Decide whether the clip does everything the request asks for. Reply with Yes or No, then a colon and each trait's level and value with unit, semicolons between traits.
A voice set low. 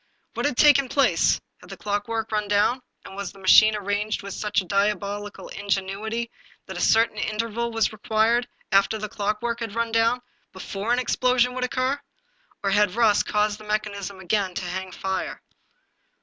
No: high, 210 Hz